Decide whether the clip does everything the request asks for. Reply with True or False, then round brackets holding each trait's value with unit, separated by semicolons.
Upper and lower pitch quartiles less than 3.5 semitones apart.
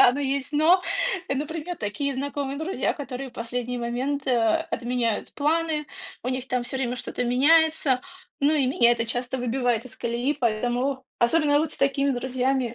True (2.9 semitones)